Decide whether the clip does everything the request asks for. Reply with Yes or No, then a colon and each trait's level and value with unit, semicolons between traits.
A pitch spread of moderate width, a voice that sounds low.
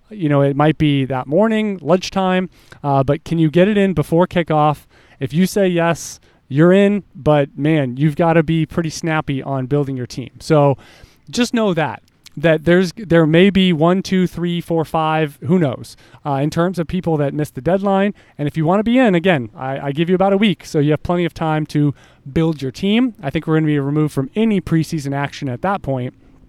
No: average, 4.2 semitones; medium, 160 Hz